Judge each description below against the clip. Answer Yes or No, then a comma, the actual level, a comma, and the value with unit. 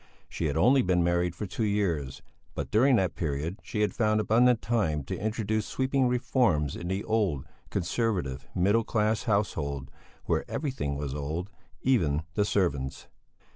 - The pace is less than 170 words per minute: Yes, average, 155 wpm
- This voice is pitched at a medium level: No, low, 100 Hz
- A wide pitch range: Yes, wide, 6.8 semitones